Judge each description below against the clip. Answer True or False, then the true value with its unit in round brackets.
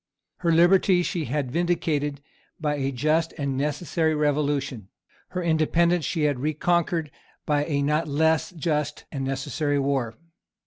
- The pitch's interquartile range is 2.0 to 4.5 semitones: True (2.7 semitones)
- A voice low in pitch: False (150 Hz)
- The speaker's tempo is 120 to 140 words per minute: True (135 wpm)